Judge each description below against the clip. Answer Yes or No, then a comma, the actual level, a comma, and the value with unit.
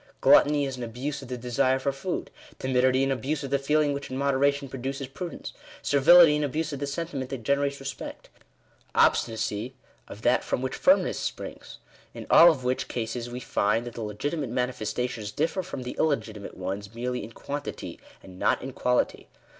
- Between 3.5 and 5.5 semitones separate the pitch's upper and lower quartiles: No, average, 2.7 semitones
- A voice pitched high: No, low, 130 Hz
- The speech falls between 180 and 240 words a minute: Yes, average, 185 wpm